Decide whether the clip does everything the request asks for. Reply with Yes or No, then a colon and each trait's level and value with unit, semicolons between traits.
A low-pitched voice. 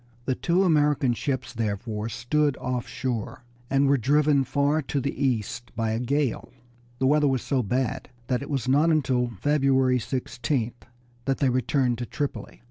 Yes: low, 130 Hz